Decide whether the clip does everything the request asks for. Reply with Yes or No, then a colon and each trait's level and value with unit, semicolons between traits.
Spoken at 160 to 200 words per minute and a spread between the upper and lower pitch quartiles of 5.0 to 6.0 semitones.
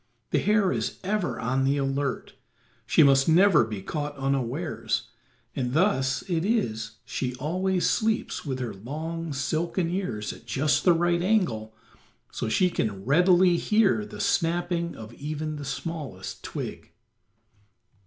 No: average, 140 wpm; average, 5.3 semitones